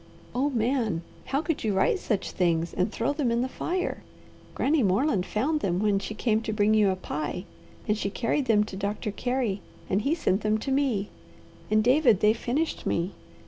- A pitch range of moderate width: Yes, average, 4.9 semitones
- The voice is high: Yes, high, 220 Hz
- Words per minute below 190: No, average, 195 wpm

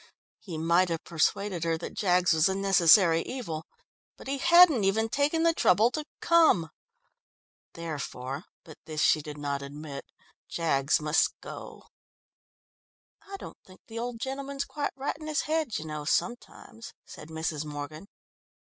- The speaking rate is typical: Yes, average, 150 wpm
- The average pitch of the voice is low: No, medium, 175 Hz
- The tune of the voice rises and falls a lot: Yes, wide, 8.2 semitones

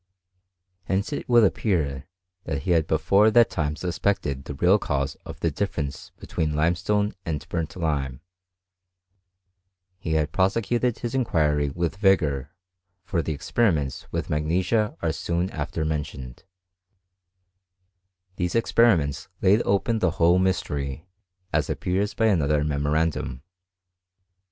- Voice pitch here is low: Yes, very low, 85 Hz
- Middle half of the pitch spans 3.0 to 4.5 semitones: No, average, 5.2 semitones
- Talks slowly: Yes, slow, 120 wpm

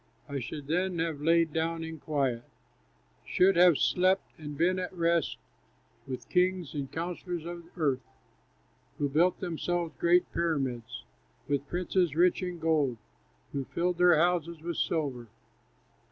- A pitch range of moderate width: Yes, average, 3.3 semitones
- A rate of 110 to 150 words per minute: Yes, average, 140 wpm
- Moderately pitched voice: Yes, medium, 165 Hz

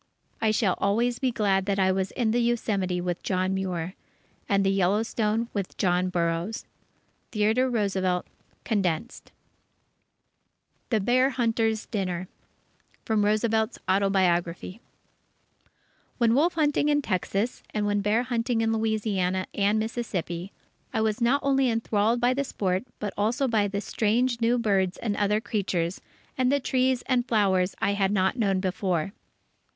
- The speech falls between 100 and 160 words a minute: Yes, average, 145 wpm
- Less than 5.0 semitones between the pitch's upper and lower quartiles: Yes, average, 3.7 semitones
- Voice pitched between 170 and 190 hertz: No, high, 210 Hz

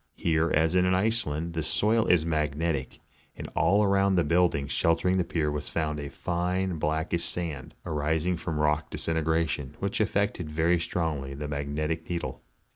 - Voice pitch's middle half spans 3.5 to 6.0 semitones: No, average, 2.9 semitones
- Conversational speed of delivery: Yes, average, 160 wpm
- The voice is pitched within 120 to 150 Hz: No, very low, 80 Hz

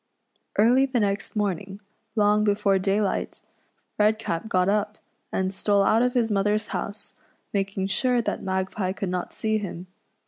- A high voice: Yes, high, 205 Hz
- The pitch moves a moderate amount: No, narrow, 2.0 semitones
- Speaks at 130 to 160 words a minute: Yes, average, 150 wpm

